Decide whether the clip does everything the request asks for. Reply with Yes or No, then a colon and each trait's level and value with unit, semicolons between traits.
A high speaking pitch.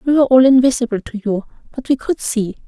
Yes: high, 245 Hz